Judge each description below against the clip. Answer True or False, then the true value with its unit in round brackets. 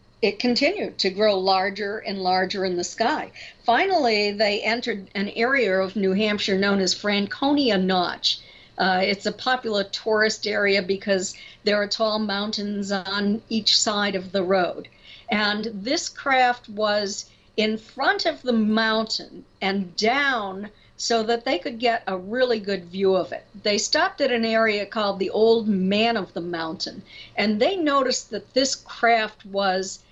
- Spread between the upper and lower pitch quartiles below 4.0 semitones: True (2.6 semitones)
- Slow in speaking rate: False (160 wpm)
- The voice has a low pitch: False (210 Hz)